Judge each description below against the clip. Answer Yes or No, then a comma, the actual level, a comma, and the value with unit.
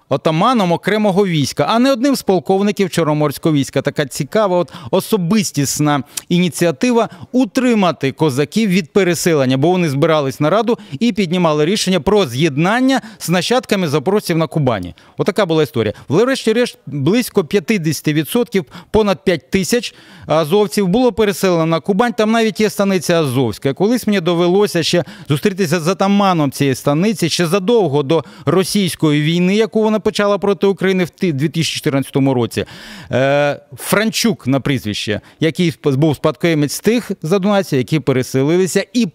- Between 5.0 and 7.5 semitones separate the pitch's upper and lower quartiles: Yes, wide, 5.4 semitones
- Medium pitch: Yes, medium, 175 Hz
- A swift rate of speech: No, average, 135 wpm